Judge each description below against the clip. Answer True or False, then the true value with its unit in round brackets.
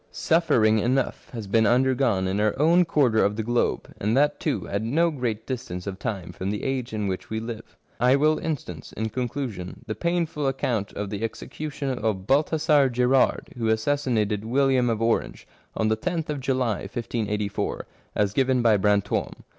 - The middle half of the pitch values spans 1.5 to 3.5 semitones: False (4.3 semitones)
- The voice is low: True (120 Hz)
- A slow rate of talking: False (180 wpm)